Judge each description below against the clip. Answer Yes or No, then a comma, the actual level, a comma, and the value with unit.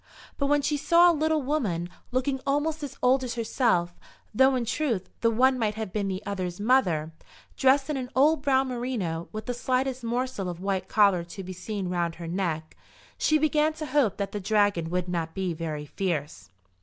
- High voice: Yes, high, 220 Hz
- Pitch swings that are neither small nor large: No, wide, 6.7 semitones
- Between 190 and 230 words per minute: Yes, average, 195 wpm